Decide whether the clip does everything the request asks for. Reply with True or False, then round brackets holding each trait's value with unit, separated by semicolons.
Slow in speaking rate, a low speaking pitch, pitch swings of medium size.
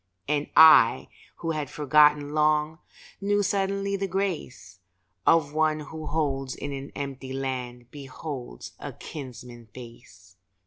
False (120 wpm; 145 Hz; 3.5 semitones)